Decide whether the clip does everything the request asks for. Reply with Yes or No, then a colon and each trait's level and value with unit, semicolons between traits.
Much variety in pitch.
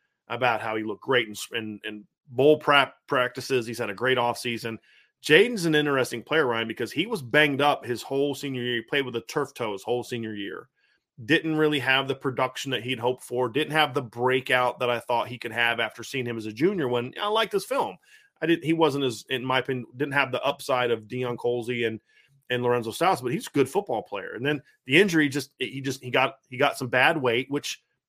No: average, 3.0 semitones